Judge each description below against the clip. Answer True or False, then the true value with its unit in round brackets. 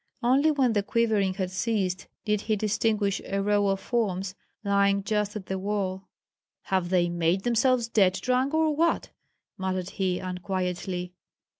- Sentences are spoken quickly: False (150 wpm)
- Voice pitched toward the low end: False (200 Hz)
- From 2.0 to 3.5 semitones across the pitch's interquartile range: True (3.2 semitones)